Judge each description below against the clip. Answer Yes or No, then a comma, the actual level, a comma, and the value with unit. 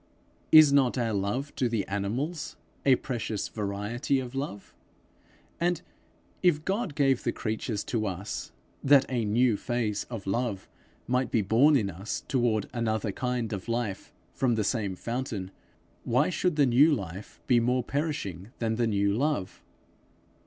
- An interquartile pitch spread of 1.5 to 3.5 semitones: No, average, 4.6 semitones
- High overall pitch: No, low, 120 Hz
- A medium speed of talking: Yes, average, 150 wpm